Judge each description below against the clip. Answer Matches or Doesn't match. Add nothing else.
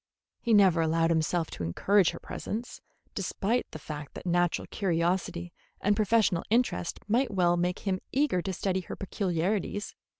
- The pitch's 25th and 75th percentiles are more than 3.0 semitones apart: Matches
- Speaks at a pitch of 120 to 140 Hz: Doesn't match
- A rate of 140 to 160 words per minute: Matches